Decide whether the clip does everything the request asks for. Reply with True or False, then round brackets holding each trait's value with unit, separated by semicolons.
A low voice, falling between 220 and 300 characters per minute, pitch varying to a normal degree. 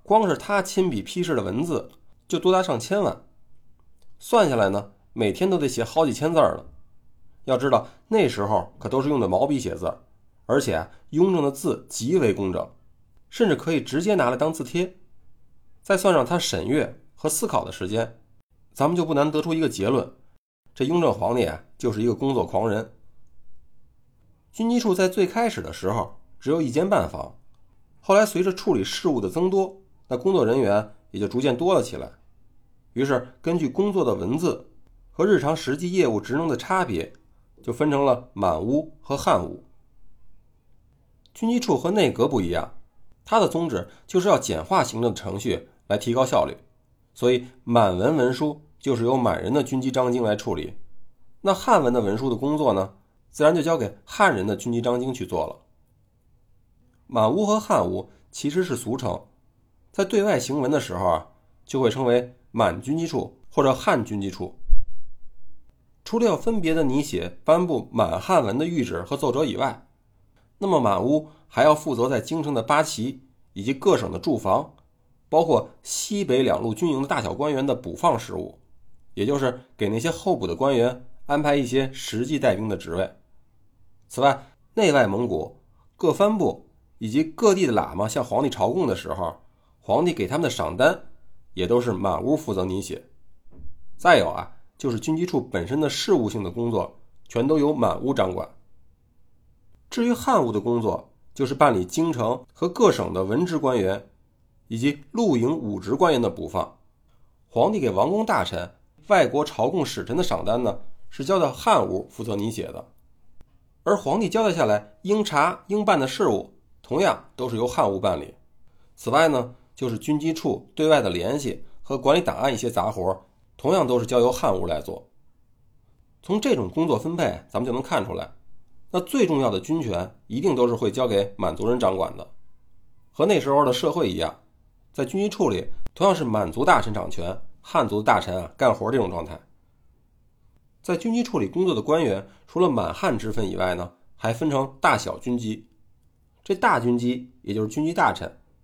False (130 Hz; 260 characters per minute; 6.9 semitones)